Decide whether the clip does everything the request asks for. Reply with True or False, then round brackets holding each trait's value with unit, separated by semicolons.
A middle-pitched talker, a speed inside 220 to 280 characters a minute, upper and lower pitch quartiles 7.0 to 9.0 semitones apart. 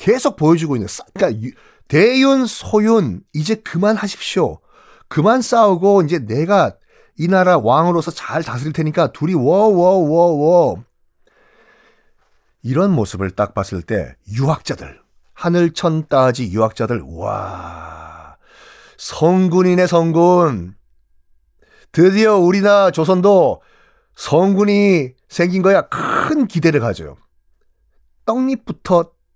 True (165 Hz; 230 characters per minute; 8.6 semitones)